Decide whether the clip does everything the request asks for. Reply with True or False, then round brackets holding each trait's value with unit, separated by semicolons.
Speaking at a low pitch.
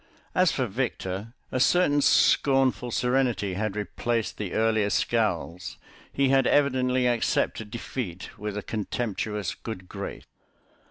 True (115 Hz)